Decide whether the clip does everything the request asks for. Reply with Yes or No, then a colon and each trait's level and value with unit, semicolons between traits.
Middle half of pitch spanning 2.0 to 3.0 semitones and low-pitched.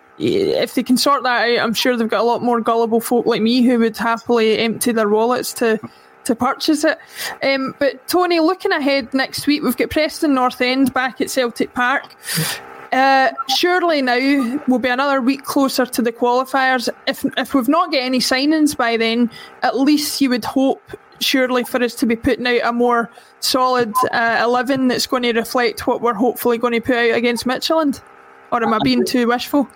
No: narrow, 2.4 semitones; very high, 255 Hz